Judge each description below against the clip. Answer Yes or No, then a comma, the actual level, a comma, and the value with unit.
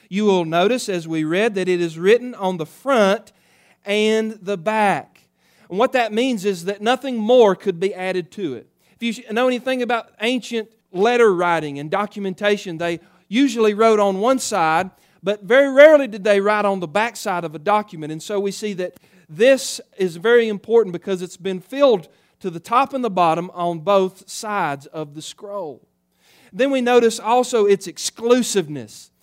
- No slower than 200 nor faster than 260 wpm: No, average, 185 wpm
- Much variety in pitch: No, average, 4.2 semitones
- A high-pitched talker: Yes, high, 205 Hz